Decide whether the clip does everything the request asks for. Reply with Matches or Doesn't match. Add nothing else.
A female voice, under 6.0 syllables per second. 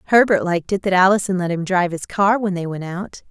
Doesn't match